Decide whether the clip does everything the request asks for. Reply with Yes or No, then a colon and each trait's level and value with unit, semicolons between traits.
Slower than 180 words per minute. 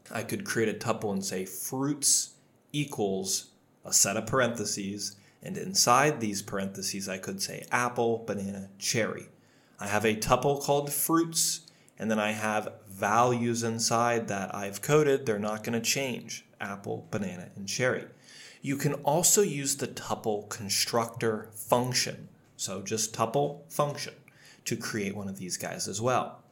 Yes: average, 150 wpm